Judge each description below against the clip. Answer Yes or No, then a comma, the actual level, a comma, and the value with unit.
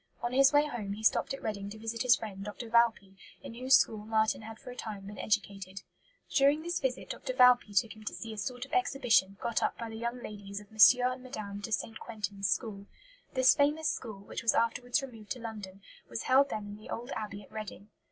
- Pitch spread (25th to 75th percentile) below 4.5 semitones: Yes, average, 3.4 semitones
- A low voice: No, high, 225 Hz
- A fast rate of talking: Yes, fast, 230 wpm